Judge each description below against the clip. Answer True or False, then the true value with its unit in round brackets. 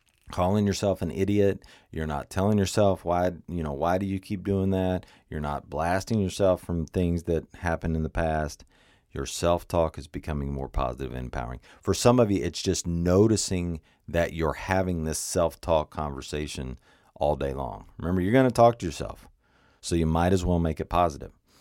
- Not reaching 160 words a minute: False (185 wpm)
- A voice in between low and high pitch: False (85 Hz)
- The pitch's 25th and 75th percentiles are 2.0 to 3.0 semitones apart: False (3.9 semitones)